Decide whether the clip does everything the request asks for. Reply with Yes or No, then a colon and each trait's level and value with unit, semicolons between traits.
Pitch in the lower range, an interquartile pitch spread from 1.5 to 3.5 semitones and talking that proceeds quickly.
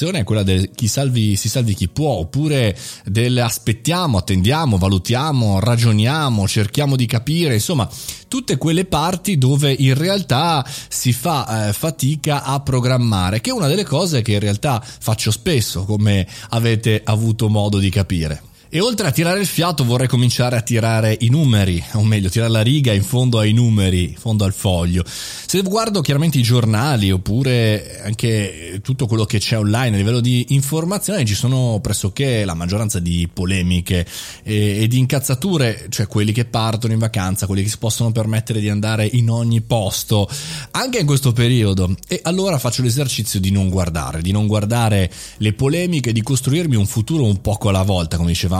No: low, 115 Hz; average, 4.6 semitones; fast, 175 wpm